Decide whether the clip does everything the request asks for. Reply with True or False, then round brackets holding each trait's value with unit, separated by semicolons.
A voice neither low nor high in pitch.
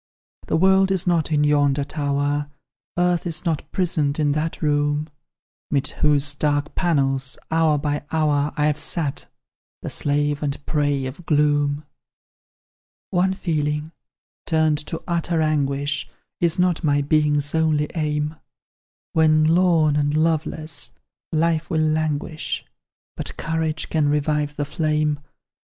True (150 Hz)